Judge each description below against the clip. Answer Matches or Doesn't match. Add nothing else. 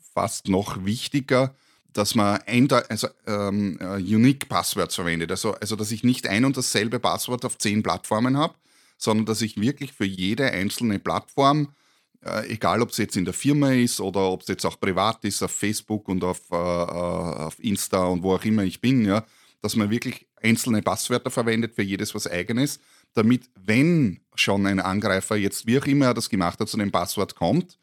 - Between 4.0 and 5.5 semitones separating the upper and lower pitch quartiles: Matches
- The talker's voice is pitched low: Matches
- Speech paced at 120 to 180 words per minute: Doesn't match